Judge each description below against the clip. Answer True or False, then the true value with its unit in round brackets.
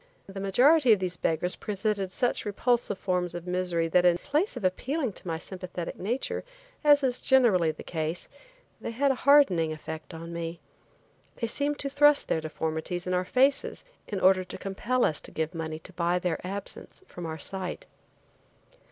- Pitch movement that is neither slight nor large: False (6.4 semitones)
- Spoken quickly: False (180 wpm)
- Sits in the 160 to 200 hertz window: True (185 Hz)